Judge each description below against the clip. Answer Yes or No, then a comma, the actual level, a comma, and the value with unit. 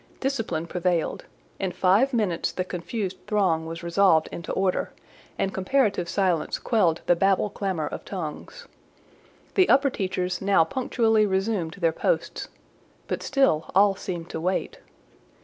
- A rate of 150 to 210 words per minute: No, slow, 135 wpm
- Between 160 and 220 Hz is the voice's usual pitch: Yes, high, 190 Hz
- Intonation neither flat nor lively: Yes, average, 3.7 semitones